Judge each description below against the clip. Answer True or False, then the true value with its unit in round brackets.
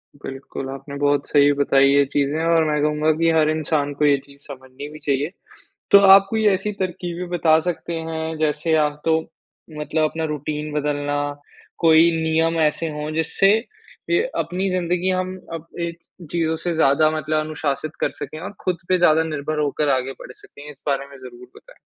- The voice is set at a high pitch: False (155 Hz)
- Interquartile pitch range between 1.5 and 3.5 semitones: True (2.5 semitones)